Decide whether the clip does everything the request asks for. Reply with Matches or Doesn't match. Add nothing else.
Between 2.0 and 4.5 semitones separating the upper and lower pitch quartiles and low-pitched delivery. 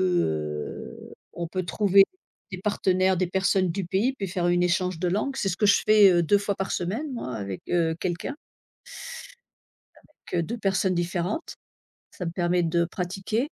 Doesn't match